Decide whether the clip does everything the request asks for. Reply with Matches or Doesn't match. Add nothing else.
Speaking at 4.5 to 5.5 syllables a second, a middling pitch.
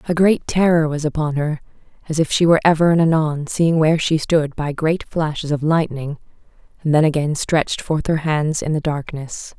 Matches